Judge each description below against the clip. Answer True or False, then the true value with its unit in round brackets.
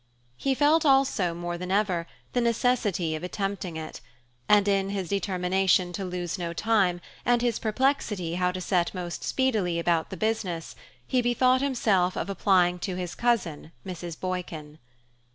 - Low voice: False (185 Hz)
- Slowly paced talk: False (155 wpm)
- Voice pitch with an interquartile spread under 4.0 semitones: False (4.3 semitones)